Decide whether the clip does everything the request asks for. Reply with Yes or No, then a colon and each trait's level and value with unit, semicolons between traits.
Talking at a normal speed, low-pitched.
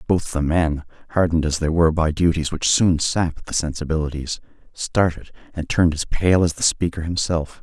Yes: average, 180 wpm; very low, 80 Hz